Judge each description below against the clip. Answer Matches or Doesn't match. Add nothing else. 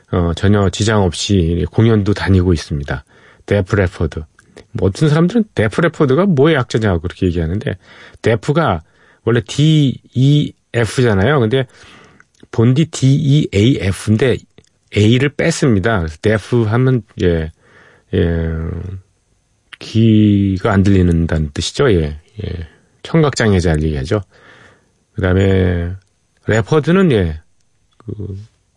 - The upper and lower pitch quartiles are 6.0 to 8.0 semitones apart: Doesn't match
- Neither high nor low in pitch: Doesn't match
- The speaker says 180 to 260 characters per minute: Matches